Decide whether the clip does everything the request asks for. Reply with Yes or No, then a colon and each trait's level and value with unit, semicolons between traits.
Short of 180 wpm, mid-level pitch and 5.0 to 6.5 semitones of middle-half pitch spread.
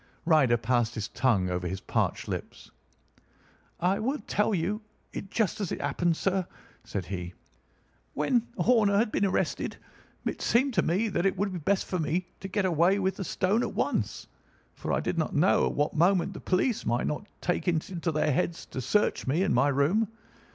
No: average, 195 wpm; medium, 175 Hz; wide, 5.6 semitones